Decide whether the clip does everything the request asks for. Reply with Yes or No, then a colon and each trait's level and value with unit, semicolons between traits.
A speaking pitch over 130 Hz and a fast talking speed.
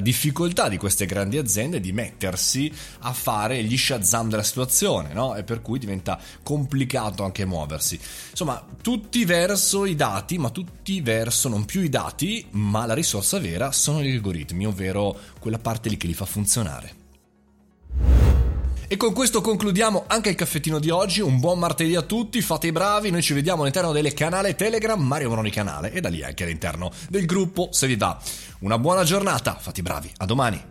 No: low, 125 Hz; fast, 180 wpm